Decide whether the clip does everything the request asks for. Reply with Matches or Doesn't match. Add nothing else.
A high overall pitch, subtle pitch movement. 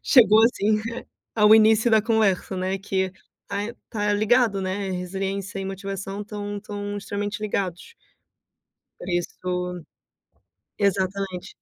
Matches